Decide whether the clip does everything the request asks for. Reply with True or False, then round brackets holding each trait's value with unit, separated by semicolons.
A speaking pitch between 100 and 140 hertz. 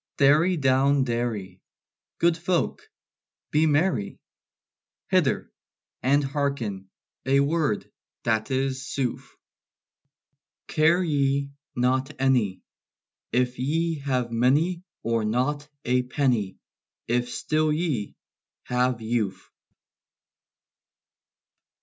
True (135 Hz)